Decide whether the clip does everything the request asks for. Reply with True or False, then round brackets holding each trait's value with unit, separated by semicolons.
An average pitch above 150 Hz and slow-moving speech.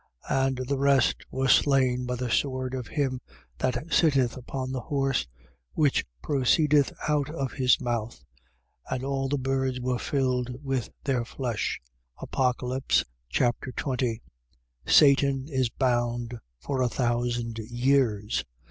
False (130 Hz; 130 wpm)